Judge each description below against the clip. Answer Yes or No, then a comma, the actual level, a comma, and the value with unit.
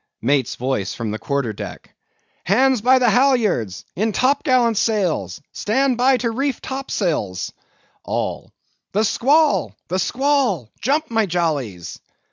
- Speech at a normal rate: No, slow, 130 wpm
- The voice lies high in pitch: Yes, high, 215 Hz